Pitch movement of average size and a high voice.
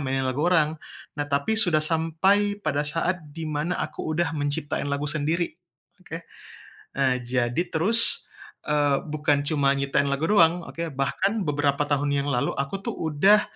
No: average, 3.0 semitones; medium, 150 Hz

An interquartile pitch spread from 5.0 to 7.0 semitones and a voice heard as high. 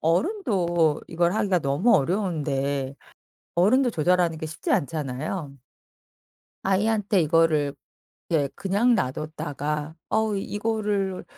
No: average, 5.3 semitones; medium, 170 Hz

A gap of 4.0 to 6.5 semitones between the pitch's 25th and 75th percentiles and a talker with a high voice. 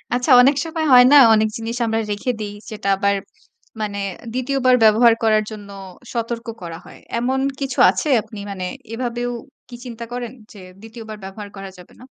No: average, 3.0 semitones; high, 225 Hz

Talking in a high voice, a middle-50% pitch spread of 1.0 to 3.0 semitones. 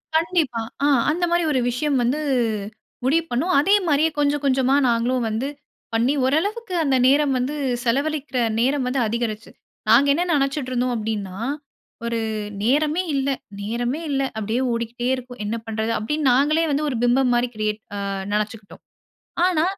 No: very high, 260 Hz; average, 4.2 semitones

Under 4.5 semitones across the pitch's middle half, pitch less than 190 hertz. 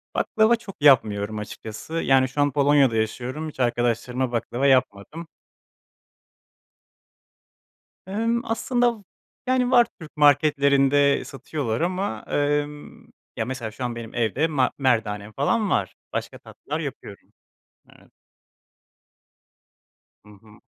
No: average, 5.1 semitones; medium, 140 Hz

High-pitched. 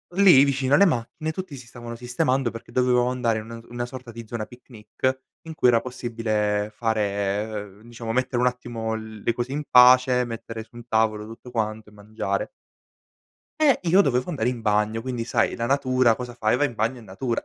No: low, 120 Hz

